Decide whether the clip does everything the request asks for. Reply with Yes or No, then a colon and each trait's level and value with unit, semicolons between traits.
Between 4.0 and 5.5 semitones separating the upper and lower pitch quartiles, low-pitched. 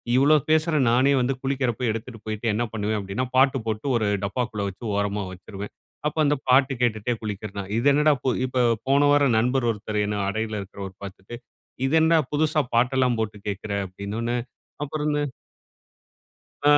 Yes: average, 4.7 semitones; low, 120 Hz